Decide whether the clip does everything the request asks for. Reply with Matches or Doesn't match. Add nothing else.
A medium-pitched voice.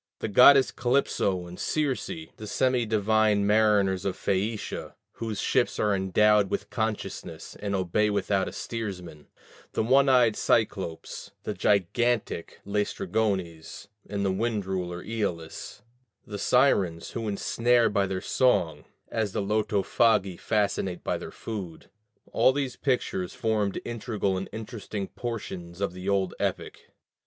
Doesn't match